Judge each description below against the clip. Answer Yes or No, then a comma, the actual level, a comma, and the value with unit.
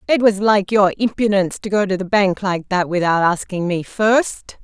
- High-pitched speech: Yes, high, 195 Hz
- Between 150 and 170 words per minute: No, fast, 205 wpm